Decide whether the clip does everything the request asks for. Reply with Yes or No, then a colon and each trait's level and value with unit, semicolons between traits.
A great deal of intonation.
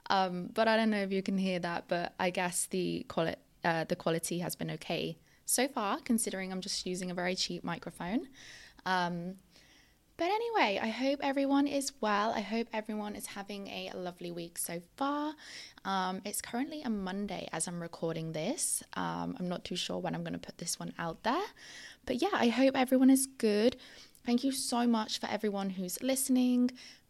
Yes: wide, 6.0 semitones